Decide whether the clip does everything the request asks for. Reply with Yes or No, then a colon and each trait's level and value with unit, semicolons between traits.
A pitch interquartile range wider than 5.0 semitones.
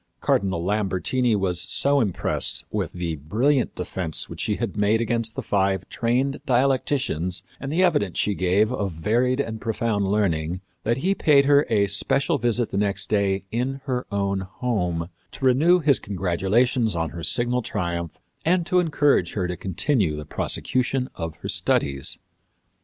Yes: wide, 5.6 semitones